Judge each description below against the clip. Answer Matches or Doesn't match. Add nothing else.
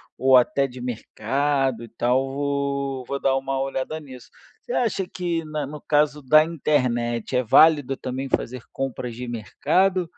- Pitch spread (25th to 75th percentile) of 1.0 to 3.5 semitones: Matches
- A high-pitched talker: Doesn't match